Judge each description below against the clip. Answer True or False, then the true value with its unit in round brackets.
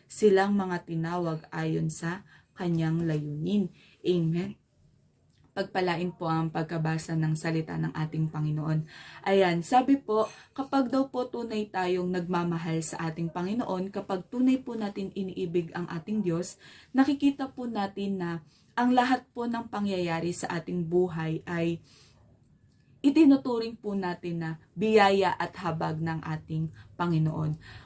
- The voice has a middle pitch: True (175 Hz)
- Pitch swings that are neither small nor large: True (4.1 semitones)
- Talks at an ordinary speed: True (130 wpm)